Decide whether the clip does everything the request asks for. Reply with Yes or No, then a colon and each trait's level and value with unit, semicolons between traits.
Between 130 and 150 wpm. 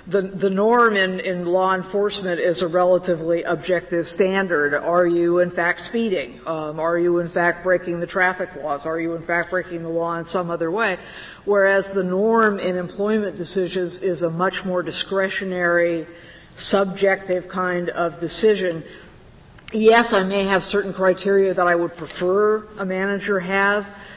No: average, 160 wpm